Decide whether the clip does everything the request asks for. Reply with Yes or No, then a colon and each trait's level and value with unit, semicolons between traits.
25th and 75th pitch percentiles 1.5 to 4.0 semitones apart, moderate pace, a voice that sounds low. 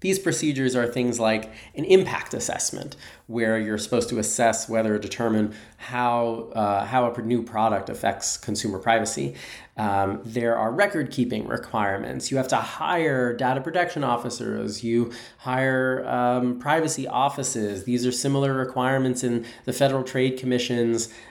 Yes: narrow, 2.6 semitones; average, 145 wpm; low, 120 Hz